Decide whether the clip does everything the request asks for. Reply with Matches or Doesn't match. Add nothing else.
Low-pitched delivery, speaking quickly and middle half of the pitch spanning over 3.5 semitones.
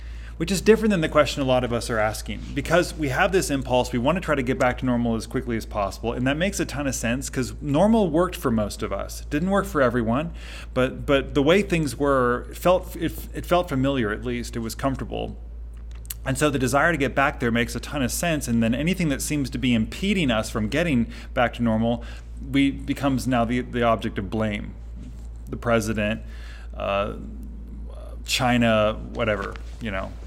Matches